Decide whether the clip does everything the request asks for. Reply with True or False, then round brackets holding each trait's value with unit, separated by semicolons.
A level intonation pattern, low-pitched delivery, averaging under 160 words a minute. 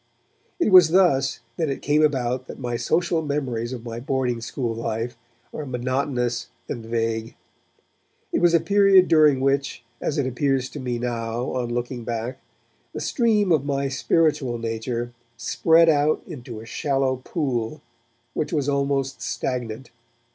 False (3.8 semitones; 130 Hz; 150 wpm)